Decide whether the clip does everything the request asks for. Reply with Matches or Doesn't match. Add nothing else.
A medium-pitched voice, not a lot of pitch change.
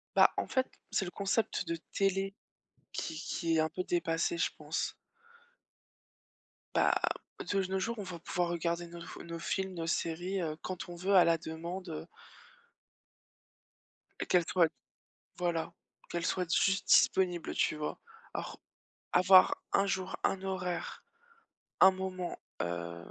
Matches